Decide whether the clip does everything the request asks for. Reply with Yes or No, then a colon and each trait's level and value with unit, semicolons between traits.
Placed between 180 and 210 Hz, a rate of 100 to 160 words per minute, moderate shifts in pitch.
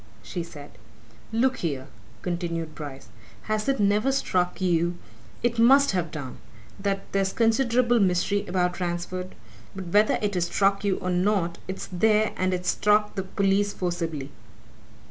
Yes: high, 190 Hz; average, 145 wpm; average, 3.3 semitones